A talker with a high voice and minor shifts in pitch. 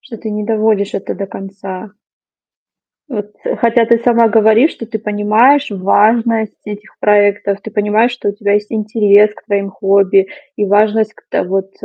Yes: high, 210 Hz; narrow, 1.7 semitones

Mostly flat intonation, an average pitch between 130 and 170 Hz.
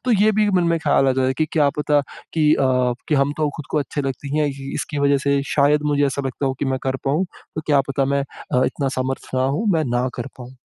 Yes: narrow, 2.1 semitones; medium, 140 Hz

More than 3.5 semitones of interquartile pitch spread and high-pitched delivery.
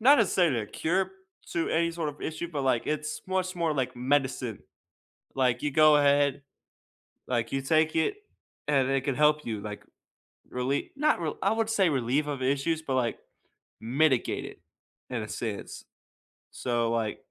No: average, 4.3 semitones; medium, 145 Hz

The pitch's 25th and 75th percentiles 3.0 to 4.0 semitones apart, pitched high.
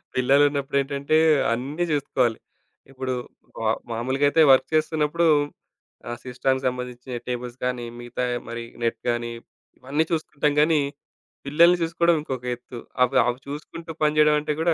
No: average, 3.4 semitones; low, 135 Hz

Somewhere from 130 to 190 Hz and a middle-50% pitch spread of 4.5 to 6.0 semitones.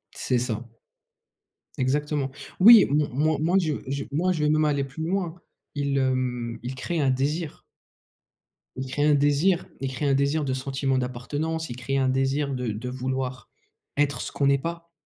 No: medium, 140 Hz; average, 2.9 semitones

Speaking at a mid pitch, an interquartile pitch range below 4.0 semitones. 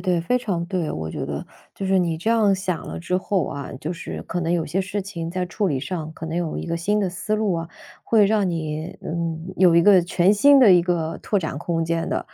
Yes: medium, 175 Hz; average, 2.9 semitones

